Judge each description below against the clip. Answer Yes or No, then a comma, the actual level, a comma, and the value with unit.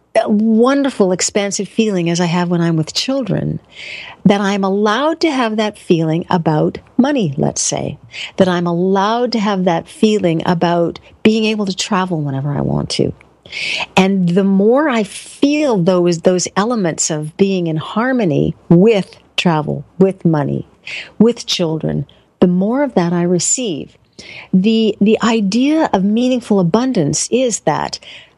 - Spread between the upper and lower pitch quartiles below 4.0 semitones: No, average, 4.3 semitones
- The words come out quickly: No, average, 145 wpm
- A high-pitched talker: Yes, high, 195 Hz